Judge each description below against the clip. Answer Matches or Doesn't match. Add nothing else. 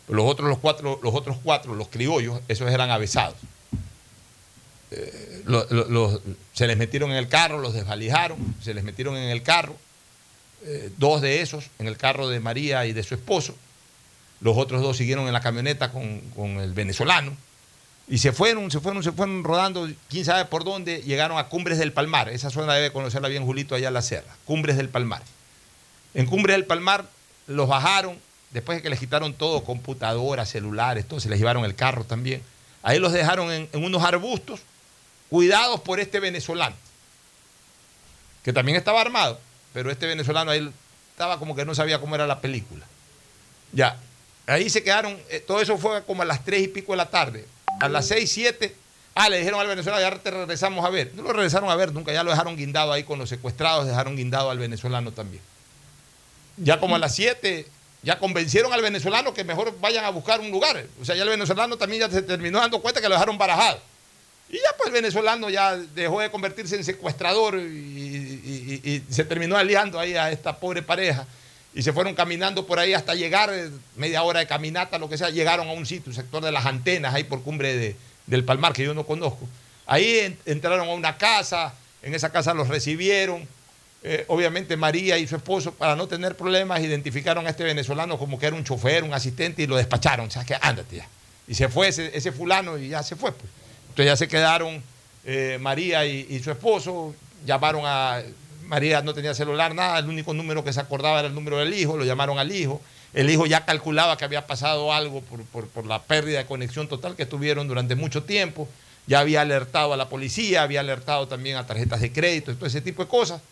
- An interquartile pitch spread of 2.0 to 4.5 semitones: Doesn't match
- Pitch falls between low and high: Matches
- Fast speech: Matches